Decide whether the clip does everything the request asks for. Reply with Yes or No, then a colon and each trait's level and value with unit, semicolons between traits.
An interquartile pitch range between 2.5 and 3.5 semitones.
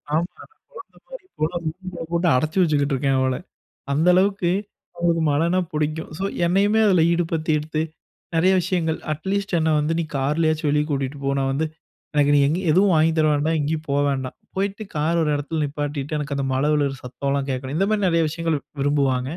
Yes: average, 3.0 semitones